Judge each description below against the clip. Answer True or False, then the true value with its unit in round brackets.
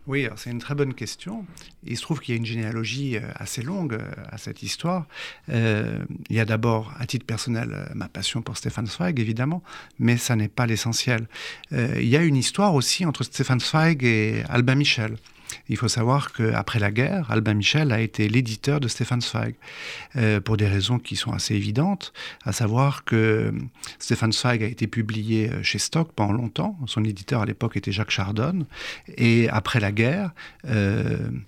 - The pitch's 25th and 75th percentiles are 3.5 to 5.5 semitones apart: True (4.2 semitones)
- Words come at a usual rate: True (185 wpm)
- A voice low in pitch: True (120 Hz)